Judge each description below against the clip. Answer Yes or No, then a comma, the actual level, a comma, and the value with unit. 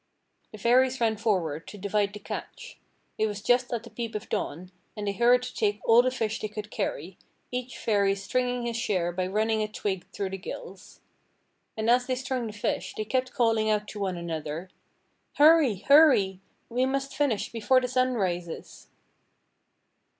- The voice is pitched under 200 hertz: No, high, 220 Hz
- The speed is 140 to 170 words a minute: No, average, 180 wpm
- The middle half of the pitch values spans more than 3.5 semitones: Yes, average, 4.0 semitones